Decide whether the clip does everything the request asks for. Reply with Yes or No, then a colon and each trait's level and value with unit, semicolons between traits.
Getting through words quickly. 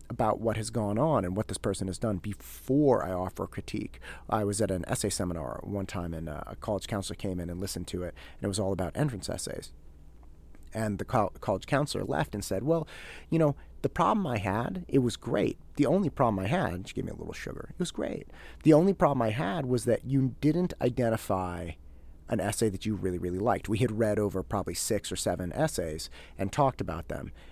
Yes: fast, 220 wpm